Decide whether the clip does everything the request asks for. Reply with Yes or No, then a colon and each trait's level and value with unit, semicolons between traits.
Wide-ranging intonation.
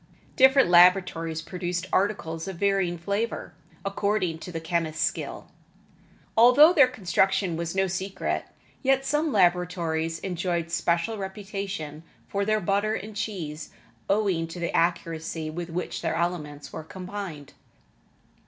No: average, 3.4 semitones